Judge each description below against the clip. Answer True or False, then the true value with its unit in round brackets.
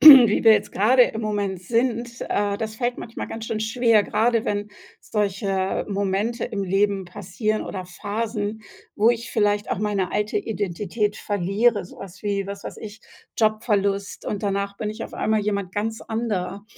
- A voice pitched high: True (210 Hz)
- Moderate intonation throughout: False (2.0 semitones)